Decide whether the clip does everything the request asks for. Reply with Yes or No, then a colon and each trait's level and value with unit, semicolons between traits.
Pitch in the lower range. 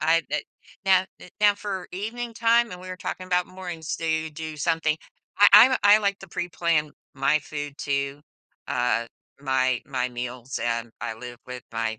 No: medium, 160 Hz